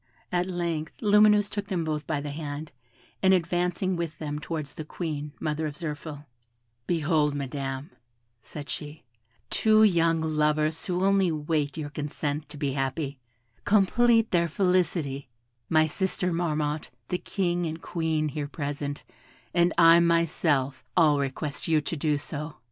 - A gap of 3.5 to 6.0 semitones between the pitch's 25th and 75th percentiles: No, average, 3.0 semitones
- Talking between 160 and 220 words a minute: No, average, 145 wpm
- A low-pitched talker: No, medium, 155 Hz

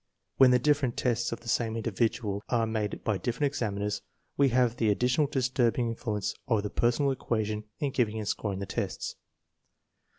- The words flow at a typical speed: Yes, average, 170 wpm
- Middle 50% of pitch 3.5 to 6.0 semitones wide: No, average, 2.9 semitones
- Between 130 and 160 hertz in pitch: No, low, 115 Hz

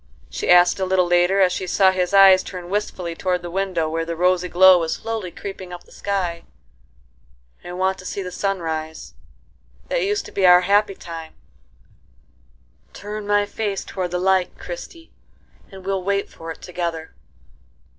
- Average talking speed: Yes, average, 165 wpm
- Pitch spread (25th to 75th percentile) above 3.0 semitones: No, narrow, 2.4 semitones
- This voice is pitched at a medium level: Yes, medium, 180 Hz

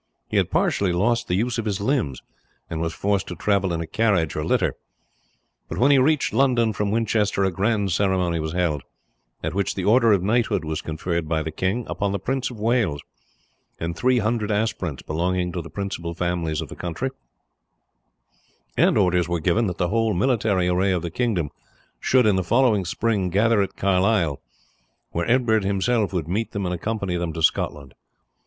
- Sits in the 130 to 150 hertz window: No, very low, 95 Hz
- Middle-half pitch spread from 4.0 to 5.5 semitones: Yes, average, 4.5 semitones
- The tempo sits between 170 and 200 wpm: Yes, average, 190 wpm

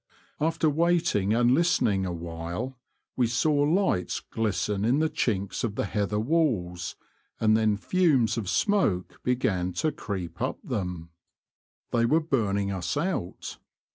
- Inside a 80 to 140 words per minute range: Yes, slow, 135 wpm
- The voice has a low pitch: Yes, low, 110 Hz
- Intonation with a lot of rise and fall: Yes, wide, 7.7 semitones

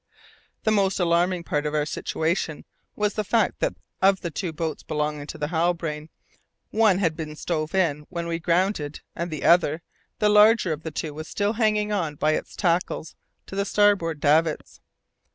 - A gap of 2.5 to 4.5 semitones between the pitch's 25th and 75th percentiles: Yes, average, 4.0 semitones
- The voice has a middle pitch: Yes, medium, 170 Hz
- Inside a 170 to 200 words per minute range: Yes, average, 180 wpm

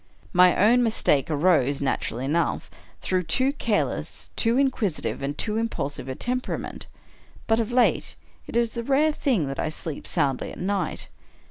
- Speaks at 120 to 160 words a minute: Yes, average, 155 wpm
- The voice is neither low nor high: No, high, 195 Hz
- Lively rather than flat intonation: Yes, wide, 8.2 semitones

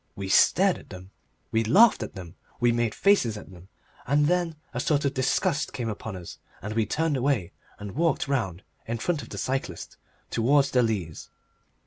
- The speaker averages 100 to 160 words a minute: No, average, 195 wpm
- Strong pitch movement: Yes, wide, 5.9 semitones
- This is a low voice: Yes, low, 120 Hz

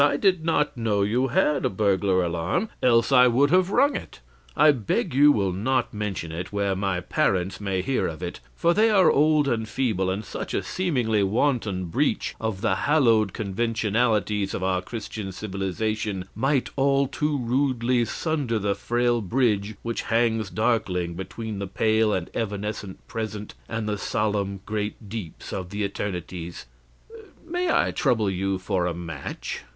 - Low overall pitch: Yes, low, 110 Hz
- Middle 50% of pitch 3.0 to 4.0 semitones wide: No, average, 4.7 semitones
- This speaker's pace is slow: No, average, 165 wpm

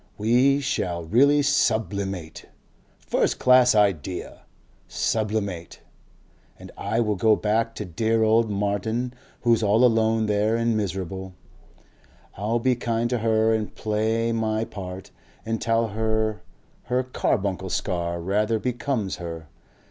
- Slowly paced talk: Yes, slow, 125 wpm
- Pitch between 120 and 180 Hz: No, low, 110 Hz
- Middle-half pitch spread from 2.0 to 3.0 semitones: Yes, narrow, 2.5 semitones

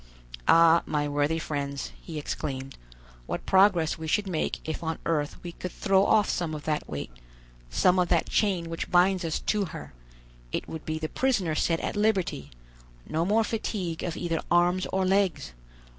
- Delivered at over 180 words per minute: No, average, 175 wpm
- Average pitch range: Yes, average, 3.3 semitones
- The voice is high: No, medium, 170 Hz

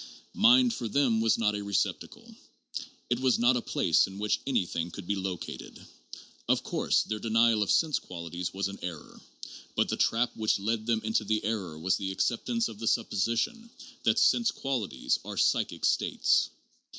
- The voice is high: No, low, 110 Hz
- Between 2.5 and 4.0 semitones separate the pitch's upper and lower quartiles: Yes, average, 3.6 semitones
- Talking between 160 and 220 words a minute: Yes, average, 175 wpm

